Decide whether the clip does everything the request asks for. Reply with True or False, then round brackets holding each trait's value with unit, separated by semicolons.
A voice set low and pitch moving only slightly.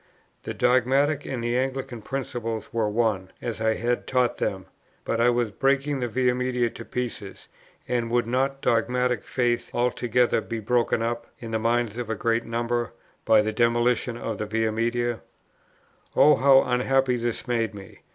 True (120 Hz; 1.6 semitones)